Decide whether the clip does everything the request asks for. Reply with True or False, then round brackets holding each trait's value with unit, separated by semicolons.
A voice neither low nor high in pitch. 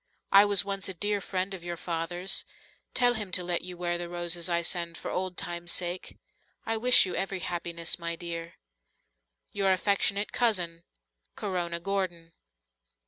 True (180 Hz)